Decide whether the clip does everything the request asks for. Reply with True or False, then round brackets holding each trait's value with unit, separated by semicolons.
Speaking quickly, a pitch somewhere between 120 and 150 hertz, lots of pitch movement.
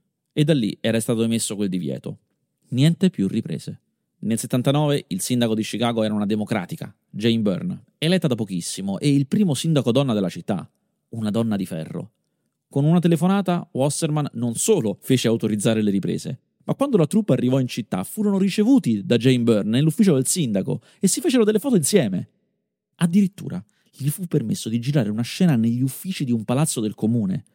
True (180 wpm; 140 Hz; 8.1 semitones)